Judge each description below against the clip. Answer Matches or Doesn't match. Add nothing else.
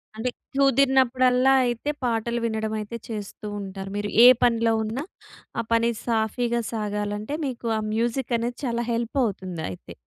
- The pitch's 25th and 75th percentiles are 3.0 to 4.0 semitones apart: Doesn't match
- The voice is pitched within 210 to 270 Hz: Matches